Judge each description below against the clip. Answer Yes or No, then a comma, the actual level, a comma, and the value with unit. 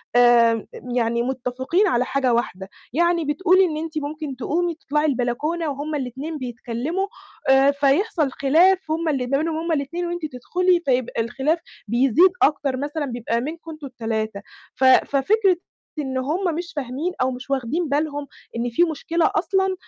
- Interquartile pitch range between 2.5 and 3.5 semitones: No, average, 4.7 semitones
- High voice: Yes, very high, 285 Hz